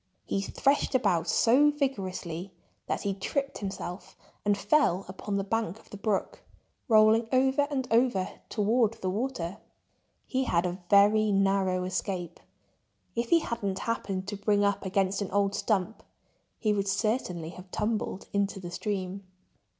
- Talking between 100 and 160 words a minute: Yes, average, 150 wpm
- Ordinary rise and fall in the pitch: Yes, average, 3.3 semitones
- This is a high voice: Yes, high, 200 Hz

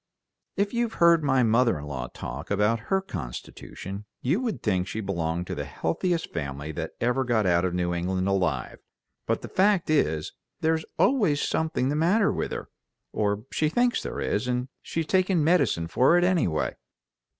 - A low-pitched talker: Yes, low, 125 Hz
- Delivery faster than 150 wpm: Yes, average, 175 wpm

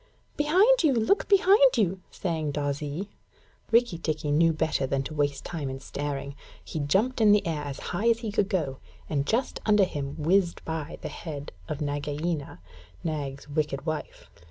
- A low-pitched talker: No, medium, 160 Hz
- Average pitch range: No, wide, 6.3 semitones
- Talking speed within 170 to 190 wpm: Yes, average, 175 wpm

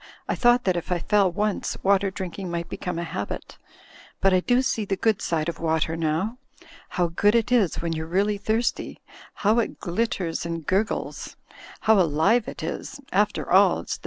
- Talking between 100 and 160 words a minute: No, average, 190 wpm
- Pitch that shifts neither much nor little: Yes, average, 4.1 semitones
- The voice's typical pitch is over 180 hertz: Yes, high, 190 Hz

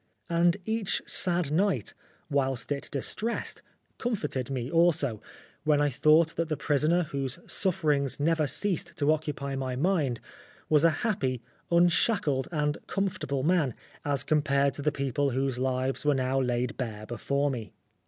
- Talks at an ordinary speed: Yes, average, 150 wpm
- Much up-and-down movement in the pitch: No, average, 3.9 semitones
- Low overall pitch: No, medium, 145 Hz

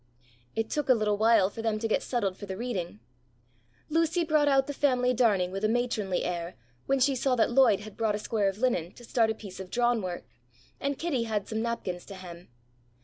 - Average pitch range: Yes, average, 4.4 semitones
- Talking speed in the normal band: No, fast, 220 wpm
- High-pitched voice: Yes, high, 225 Hz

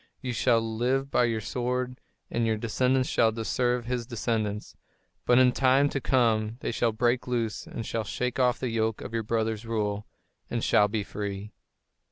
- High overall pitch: No, low, 115 Hz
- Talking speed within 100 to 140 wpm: No, average, 180 wpm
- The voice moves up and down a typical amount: No, narrow, 2.2 semitones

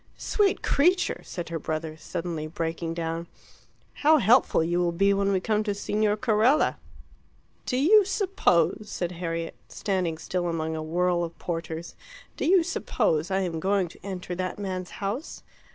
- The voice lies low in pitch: No, medium, 180 Hz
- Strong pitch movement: No, average, 4.1 semitones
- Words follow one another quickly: No, average, 160 wpm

